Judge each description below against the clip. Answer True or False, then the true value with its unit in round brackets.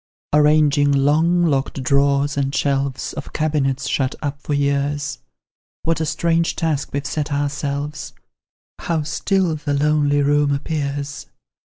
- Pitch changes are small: True (1.5 semitones)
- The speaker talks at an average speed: False (130 wpm)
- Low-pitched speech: False (145 Hz)